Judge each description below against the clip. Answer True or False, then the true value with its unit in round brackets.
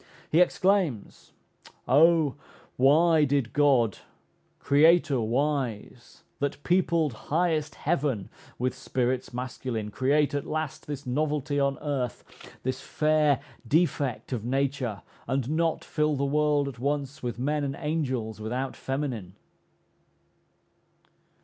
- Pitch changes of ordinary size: True (3.1 semitones)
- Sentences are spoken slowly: True (110 wpm)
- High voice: False (140 Hz)